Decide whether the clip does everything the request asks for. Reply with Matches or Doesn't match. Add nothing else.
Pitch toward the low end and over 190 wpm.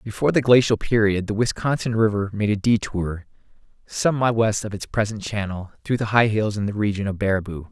Matches